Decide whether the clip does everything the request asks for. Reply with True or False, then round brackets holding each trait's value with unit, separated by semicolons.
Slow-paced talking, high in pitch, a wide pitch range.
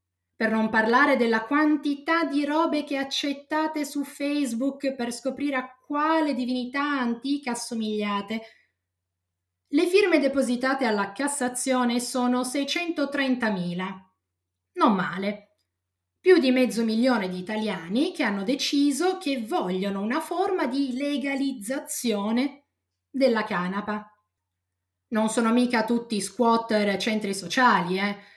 True (110 wpm; 245 Hz; 5.7 semitones)